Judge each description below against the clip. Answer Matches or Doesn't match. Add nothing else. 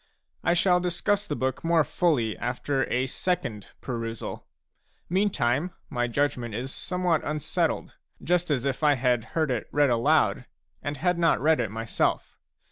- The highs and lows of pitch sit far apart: Matches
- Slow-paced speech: Doesn't match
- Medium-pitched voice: Matches